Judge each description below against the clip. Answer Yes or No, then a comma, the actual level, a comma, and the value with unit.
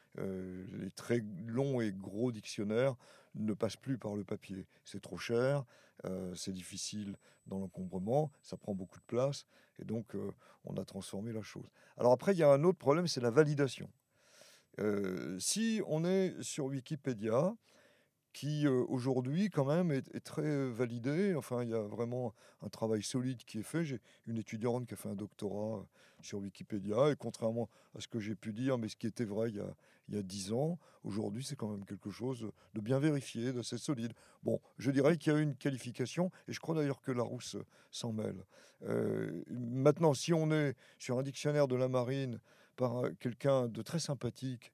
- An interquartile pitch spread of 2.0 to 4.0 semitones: No, average, 4.7 semitones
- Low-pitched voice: Yes, low, 120 Hz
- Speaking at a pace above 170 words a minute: Yes, average, 190 wpm